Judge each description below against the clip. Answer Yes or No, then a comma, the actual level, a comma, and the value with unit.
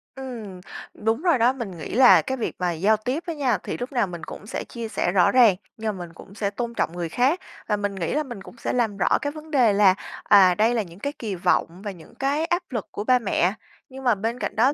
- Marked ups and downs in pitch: No, average, 4.9 semitones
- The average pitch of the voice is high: Yes, high, 225 Hz